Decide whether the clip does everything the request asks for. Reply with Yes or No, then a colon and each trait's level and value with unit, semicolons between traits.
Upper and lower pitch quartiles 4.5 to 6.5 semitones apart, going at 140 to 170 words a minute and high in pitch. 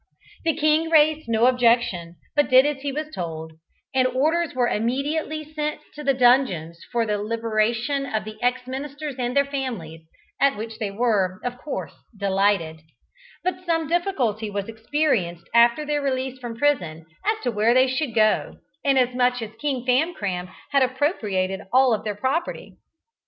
Yes: average, 5.2 semitones; average, 160 wpm; very high, 250 Hz